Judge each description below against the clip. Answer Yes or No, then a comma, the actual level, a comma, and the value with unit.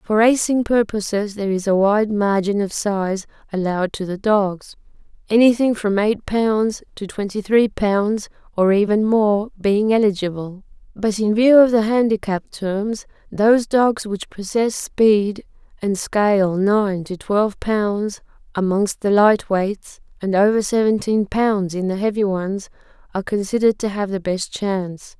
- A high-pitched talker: Yes, high, 205 Hz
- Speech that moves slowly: No, average, 150 wpm